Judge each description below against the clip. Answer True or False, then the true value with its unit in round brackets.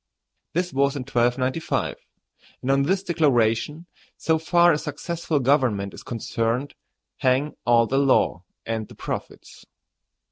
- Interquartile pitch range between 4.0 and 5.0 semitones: True (4.6 semitones)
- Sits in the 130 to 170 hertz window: True (135 Hz)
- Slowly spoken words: True (130 wpm)